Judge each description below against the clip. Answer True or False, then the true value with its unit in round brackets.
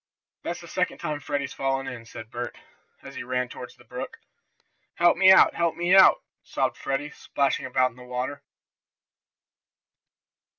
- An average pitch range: True (3.3 semitones)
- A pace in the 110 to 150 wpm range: False (160 wpm)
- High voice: False (135 Hz)